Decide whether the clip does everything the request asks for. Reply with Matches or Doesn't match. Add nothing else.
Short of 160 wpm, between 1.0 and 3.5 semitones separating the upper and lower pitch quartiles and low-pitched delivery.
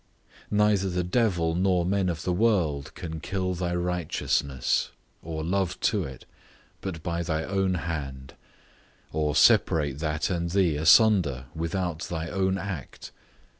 Matches